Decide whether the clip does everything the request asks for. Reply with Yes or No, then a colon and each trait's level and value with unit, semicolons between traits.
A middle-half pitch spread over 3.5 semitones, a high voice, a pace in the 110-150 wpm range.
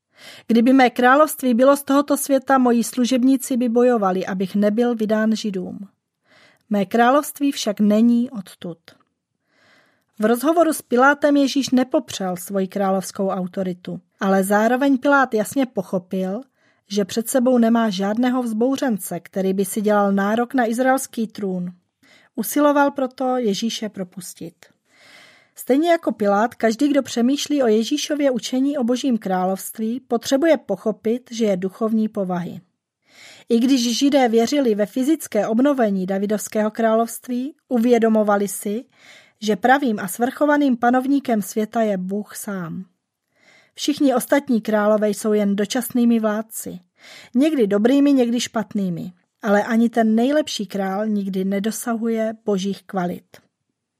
Yes: average, 4.2 semitones; high, 230 Hz; average, 120 wpm